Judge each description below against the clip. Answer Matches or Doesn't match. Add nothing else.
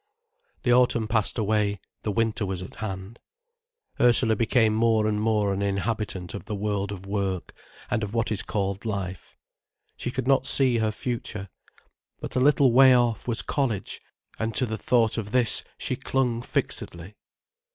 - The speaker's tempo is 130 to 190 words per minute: Matches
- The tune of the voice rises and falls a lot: Doesn't match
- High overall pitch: Doesn't match